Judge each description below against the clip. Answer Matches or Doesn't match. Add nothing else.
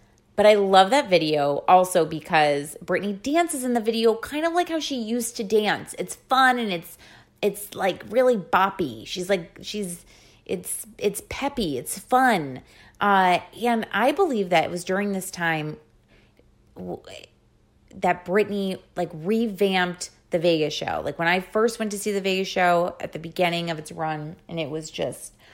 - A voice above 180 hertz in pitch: Matches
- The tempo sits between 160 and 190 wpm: Matches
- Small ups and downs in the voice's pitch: Doesn't match